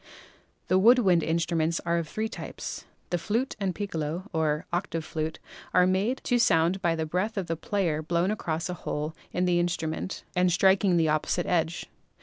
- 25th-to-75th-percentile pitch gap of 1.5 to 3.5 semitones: Yes, average, 2.8 semitones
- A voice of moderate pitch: Yes, medium, 175 Hz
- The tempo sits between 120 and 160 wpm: No, average, 185 wpm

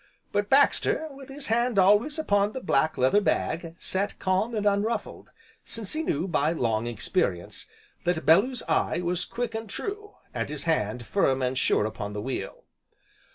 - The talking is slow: No, average, 165 wpm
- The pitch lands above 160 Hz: Yes, high, 190 Hz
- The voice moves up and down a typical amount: No, wide, 8.5 semitones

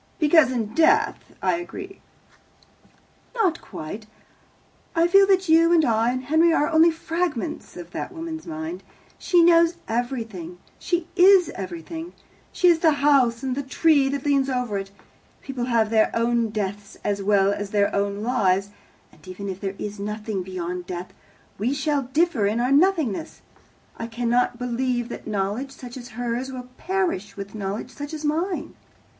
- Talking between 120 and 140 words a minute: No, average, 160 wpm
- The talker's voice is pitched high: Yes, very high, 250 Hz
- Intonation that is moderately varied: No, wide, 7.6 semitones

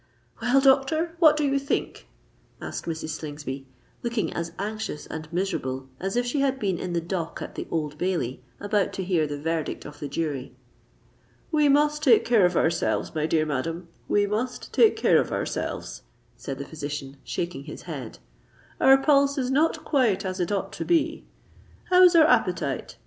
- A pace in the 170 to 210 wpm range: Yes, average, 175 wpm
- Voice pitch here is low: No, high, 190 Hz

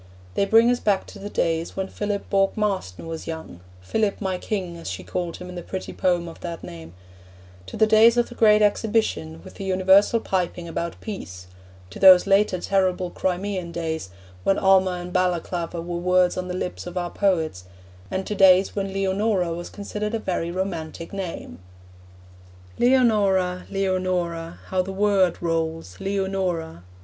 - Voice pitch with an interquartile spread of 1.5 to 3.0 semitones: Yes, narrow, 2.6 semitones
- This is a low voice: No, medium, 185 Hz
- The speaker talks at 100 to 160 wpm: No, average, 170 wpm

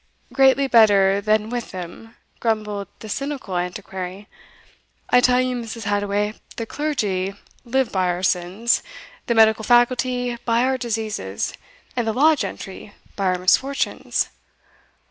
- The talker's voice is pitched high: Yes, high, 220 Hz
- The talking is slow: Yes, slow, 130 wpm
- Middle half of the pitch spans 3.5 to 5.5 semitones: Yes, average, 4.0 semitones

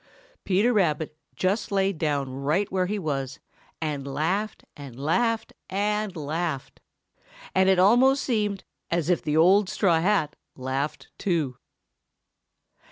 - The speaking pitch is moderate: Yes, medium, 175 Hz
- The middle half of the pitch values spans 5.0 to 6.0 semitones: Yes, wide, 5.4 semitones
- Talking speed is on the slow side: Yes, slow, 125 wpm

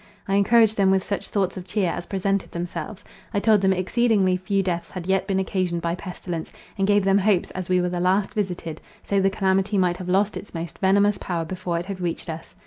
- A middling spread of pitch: No, narrow, 1.9 semitones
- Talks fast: Yes, fast, 225 wpm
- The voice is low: No, high, 190 Hz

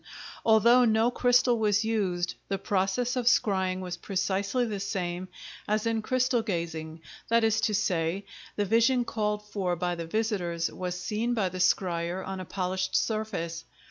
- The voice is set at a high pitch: Yes, high, 200 Hz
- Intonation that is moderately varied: Yes, average, 3.8 semitones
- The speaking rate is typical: Yes, average, 155 wpm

